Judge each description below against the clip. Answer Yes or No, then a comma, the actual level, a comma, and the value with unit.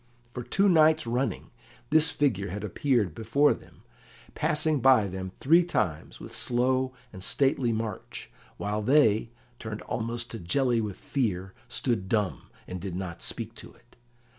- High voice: No, low, 115 Hz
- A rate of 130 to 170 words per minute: Yes, average, 150 wpm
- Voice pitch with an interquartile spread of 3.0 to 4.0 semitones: No, average, 4.8 semitones